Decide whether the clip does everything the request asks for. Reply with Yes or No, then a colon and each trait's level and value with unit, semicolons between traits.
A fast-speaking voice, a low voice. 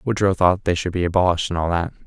Yes: fast, 260 wpm; very low, 90 Hz